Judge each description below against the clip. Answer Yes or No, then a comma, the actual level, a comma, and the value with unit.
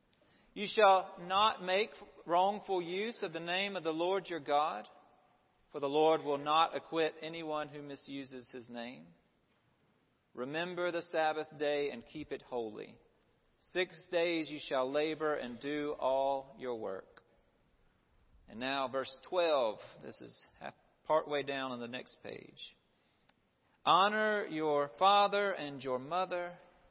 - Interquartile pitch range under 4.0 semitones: No, average, 4.6 semitones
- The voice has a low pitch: No, medium, 155 Hz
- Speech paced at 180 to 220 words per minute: No, average, 140 wpm